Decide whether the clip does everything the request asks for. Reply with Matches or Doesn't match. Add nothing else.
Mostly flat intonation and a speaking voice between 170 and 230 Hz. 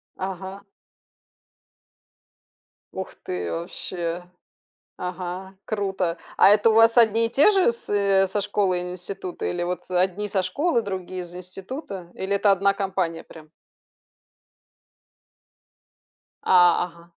Matches